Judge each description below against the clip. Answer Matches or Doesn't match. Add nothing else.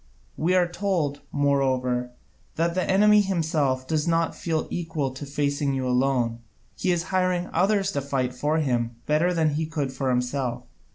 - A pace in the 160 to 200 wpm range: Matches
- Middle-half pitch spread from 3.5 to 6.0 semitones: Matches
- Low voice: Doesn't match